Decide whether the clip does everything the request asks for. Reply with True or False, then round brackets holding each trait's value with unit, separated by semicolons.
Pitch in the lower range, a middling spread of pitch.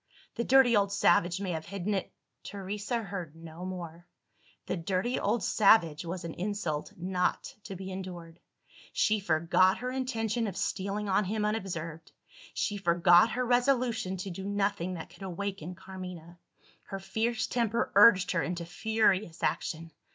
False (190 Hz; 3.4 semitones)